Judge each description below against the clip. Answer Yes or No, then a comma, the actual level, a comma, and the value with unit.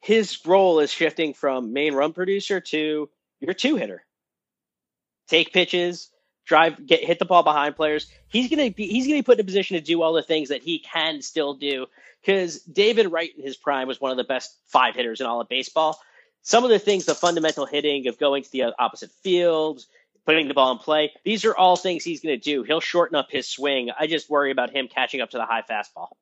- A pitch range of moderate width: Yes, average, 4.4 semitones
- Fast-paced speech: Yes, fast, 225 wpm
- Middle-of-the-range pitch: Yes, medium, 160 Hz